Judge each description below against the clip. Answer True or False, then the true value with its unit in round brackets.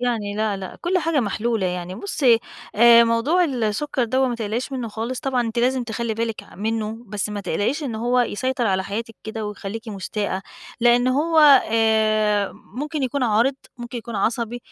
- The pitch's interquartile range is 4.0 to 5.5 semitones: False (2.9 semitones)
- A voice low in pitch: False (230 Hz)